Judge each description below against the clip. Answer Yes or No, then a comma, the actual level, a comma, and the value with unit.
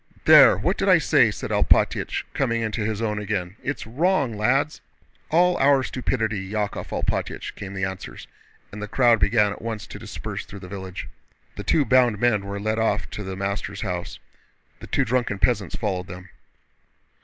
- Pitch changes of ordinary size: Yes, average, 3.4 semitones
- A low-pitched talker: Yes, low, 105 Hz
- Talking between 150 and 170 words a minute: No, average, 180 wpm